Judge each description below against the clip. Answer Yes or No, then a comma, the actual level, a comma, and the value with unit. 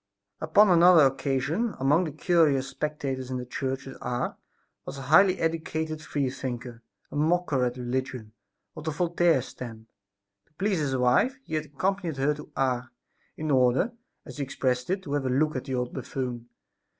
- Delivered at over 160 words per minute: Yes, average, 175 wpm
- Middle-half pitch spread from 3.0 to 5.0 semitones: Yes, average, 3.8 semitones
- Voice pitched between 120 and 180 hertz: Yes, medium, 140 Hz